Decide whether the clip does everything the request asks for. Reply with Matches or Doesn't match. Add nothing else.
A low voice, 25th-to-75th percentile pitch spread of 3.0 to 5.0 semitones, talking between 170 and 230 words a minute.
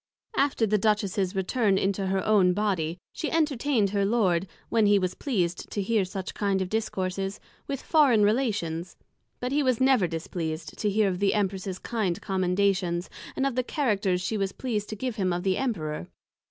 Doesn't match